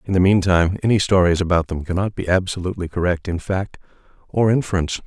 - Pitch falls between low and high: No, very low, 90 Hz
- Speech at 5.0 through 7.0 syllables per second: Yes, 6.6 syllables/s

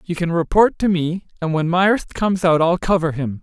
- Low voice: No, medium, 175 Hz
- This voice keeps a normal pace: No, fast, 230 wpm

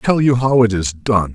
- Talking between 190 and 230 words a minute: No, fast, 265 wpm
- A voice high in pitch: No, low, 115 Hz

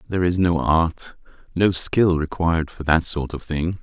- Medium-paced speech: Yes, average, 190 wpm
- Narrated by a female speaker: No, male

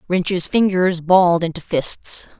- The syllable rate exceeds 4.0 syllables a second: No, 3.8 syllables/s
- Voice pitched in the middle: Yes, medium, 175 Hz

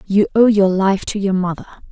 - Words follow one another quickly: Yes, fast, 220 wpm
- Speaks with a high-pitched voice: Yes, high, 195 Hz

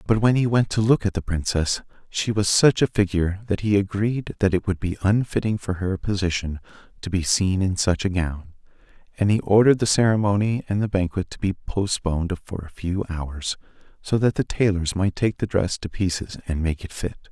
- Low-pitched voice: Yes, very low, 95 Hz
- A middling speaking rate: No, fast, 210 wpm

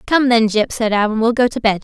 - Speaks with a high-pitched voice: Yes, high, 230 Hz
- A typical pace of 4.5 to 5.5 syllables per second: No, 5.9 syllables/s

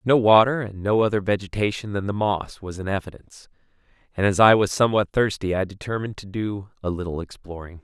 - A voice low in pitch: Yes, low, 100 Hz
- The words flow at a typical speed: Yes, average, 190 wpm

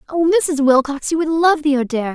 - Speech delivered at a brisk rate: Yes, fast, 225 wpm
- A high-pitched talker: Yes, very high, 295 Hz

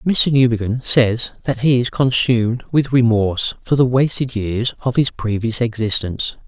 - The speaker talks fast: No, average, 160 wpm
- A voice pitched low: Yes, low, 120 Hz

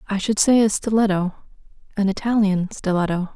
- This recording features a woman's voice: Yes, female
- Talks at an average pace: No, slow, 125 wpm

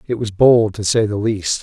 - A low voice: Yes, low, 110 Hz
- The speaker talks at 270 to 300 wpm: No, fast, 260 wpm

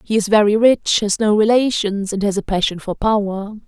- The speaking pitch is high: Yes, high, 210 Hz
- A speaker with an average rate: No, fast, 210 wpm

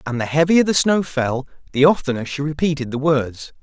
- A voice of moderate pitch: Yes, medium, 145 Hz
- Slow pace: No, average, 200 wpm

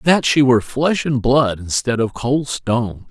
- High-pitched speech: No, low, 125 Hz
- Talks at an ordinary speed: Yes, average, 195 wpm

